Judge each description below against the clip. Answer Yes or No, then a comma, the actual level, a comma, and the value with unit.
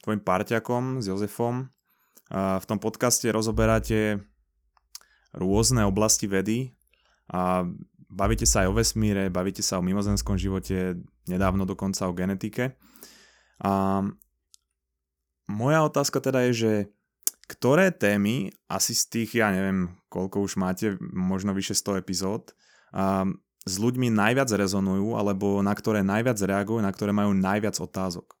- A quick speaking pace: No, average, 130 wpm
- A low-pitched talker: Yes, low, 100 Hz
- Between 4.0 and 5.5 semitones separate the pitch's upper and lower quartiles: No, average, 2.8 semitones